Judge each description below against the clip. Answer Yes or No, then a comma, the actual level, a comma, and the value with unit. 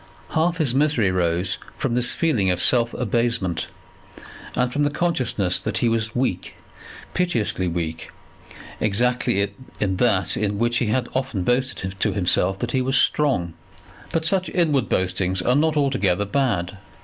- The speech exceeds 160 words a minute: No, average, 150 wpm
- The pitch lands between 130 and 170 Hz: No, low, 115 Hz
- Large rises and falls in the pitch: Yes, wide, 6.0 semitones